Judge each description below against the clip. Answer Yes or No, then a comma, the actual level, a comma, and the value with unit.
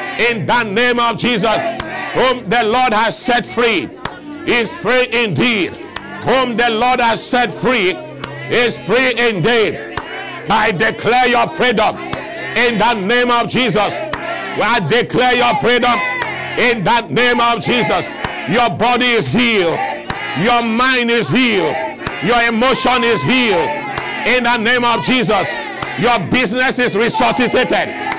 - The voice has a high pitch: Yes, high, 240 Hz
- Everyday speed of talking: No, slow, 130 wpm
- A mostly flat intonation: Yes, narrow, 1.1 semitones